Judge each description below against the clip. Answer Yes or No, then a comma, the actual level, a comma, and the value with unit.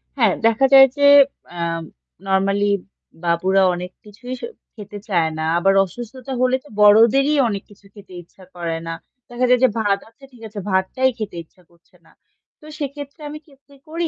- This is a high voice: Yes, high, 210 Hz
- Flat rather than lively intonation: No, wide, 5.6 semitones